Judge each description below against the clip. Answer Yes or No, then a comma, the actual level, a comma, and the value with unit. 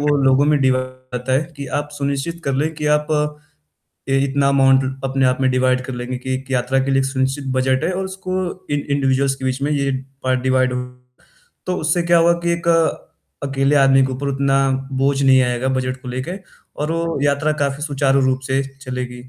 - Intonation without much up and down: Yes, narrow, 1.7 semitones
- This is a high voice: No, low, 135 Hz